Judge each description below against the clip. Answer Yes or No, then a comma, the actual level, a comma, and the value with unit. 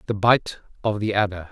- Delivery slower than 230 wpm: Yes, average, 200 wpm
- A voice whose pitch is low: Yes, low, 100 Hz